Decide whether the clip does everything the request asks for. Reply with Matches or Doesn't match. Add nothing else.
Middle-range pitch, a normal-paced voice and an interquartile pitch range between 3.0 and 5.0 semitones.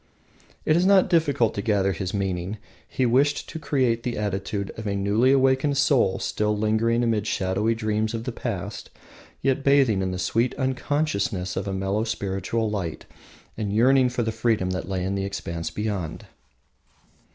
Doesn't match